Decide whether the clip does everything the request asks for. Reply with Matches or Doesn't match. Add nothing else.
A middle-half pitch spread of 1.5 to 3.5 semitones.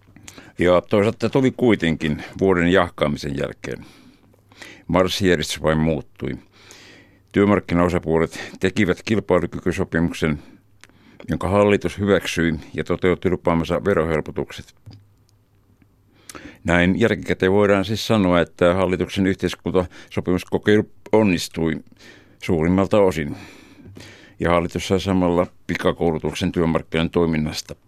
Matches